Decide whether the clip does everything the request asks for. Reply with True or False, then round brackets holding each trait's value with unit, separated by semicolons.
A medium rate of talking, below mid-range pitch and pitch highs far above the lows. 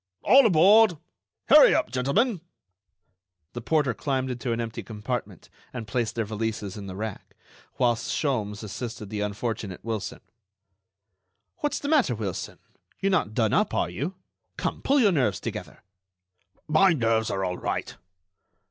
True (145 wpm; 115 Hz; 6.7 semitones)